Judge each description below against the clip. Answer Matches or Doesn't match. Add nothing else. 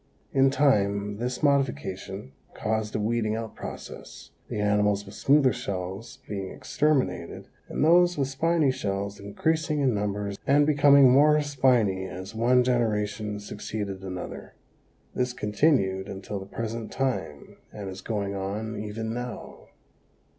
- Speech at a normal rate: Doesn't match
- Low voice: Matches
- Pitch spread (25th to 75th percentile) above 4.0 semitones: Matches